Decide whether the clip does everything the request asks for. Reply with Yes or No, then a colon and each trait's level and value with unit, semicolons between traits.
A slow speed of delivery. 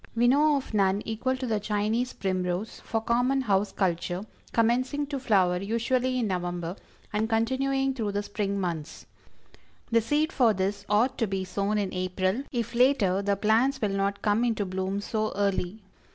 No: average, 170 wpm